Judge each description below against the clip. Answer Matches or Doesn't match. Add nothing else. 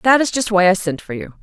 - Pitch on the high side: Matches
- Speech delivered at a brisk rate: Matches